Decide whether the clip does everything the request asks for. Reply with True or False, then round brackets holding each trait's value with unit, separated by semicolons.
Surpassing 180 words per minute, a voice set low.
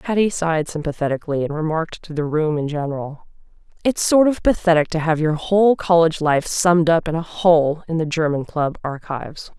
False (190 wpm; 160 Hz)